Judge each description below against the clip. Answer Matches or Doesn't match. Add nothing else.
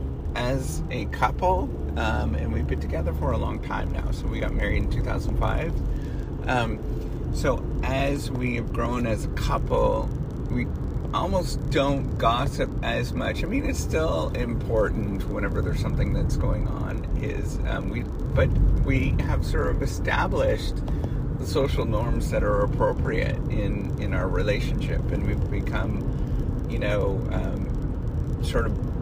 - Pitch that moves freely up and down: Matches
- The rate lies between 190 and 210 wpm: Doesn't match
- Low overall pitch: Matches